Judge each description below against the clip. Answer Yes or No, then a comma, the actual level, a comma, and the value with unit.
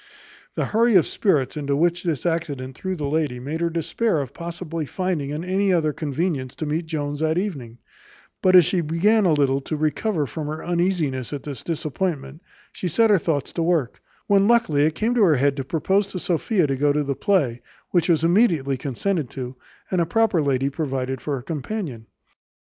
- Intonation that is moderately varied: Yes, average, 4.5 semitones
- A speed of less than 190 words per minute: No, average, 195 wpm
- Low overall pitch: No, medium, 160 Hz